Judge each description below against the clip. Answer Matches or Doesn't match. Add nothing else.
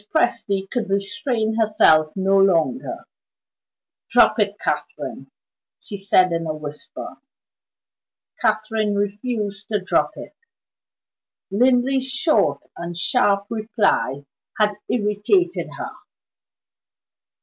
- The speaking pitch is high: Matches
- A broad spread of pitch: Doesn't match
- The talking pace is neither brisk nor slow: Doesn't match